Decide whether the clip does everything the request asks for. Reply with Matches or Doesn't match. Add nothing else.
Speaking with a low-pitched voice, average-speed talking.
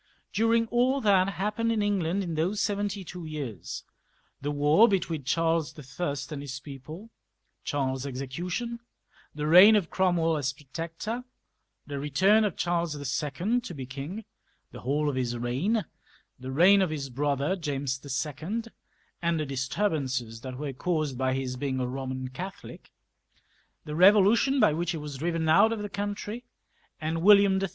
Doesn't match